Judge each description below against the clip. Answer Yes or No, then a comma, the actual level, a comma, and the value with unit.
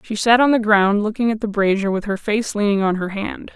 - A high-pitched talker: Yes, high, 210 Hz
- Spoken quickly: Yes, fast, 270 wpm